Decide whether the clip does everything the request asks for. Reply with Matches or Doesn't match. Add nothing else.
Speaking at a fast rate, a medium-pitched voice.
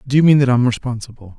Doesn't match